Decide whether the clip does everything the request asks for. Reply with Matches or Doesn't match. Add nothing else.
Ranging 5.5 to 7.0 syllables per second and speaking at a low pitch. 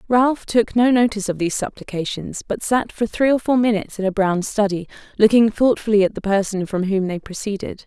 Doesn't match